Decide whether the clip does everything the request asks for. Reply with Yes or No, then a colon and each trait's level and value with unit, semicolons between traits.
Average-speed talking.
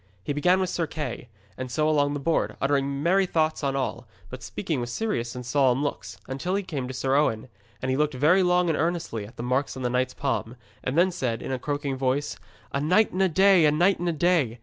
No: fast, 240 wpm